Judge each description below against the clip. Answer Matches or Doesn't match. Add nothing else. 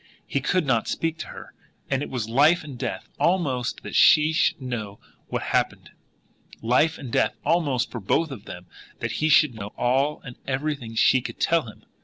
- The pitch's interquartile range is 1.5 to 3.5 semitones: Doesn't match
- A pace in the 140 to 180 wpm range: Doesn't match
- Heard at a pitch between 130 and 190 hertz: Matches